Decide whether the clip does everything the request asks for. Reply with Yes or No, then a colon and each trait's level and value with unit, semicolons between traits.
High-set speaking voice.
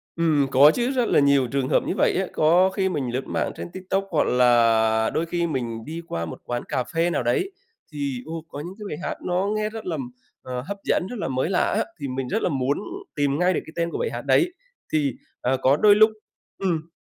No: medium, 155 Hz